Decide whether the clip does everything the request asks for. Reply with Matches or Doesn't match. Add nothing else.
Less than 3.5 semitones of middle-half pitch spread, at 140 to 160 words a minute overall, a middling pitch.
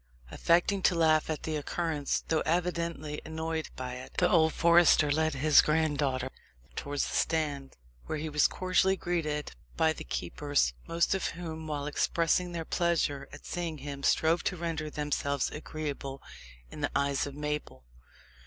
Matches